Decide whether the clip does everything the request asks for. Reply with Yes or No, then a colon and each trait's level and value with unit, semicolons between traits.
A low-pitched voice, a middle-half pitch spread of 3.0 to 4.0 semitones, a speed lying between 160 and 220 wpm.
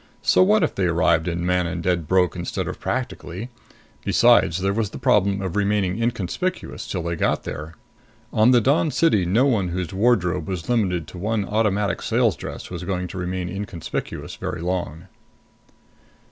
Yes: very low, 95 Hz; average, 3.7 semitones; average, 170 wpm